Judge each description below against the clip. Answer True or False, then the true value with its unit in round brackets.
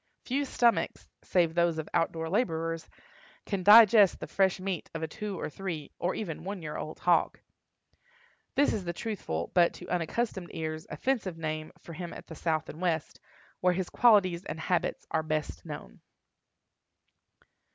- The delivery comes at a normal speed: True (165 wpm)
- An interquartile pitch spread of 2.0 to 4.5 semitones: True (3.5 semitones)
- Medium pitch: True (175 Hz)